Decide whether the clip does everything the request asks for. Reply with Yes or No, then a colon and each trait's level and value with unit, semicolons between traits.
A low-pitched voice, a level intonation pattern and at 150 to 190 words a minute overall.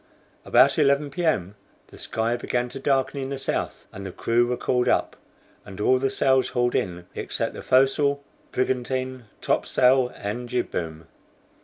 Yes: low, 125 Hz; narrow, 2.1 semitones; average, 170 wpm